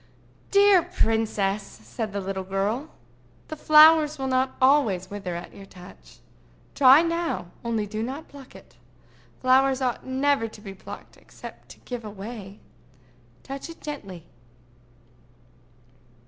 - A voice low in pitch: No, high, 240 Hz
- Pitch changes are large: Yes, wide, 6.4 semitones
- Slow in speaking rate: Yes, slow, 125 wpm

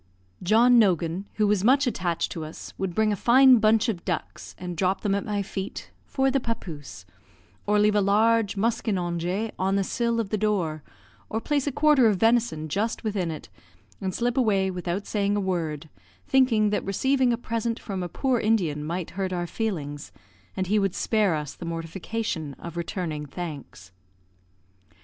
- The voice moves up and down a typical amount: Yes, average, 4.5 semitones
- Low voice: No, high, 200 Hz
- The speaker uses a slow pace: No, average, 175 wpm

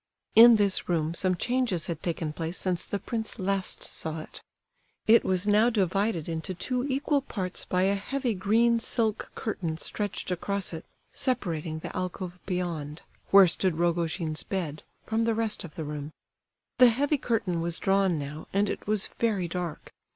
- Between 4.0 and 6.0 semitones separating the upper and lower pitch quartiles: Yes, average, 4.8 semitones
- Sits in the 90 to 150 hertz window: No, medium, 185 Hz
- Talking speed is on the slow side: No, average, 165 wpm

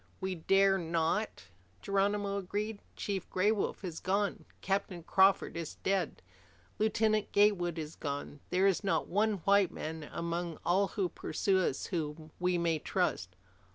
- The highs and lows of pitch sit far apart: No, average, 3.1 semitones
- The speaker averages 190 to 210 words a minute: No, average, 145 wpm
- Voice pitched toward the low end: No, high, 190 Hz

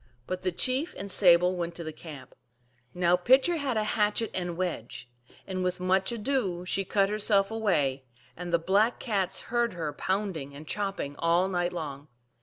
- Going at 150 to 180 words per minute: Yes, average, 175 wpm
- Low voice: No, medium, 185 Hz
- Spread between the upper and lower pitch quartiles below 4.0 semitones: Yes, average, 3.6 semitones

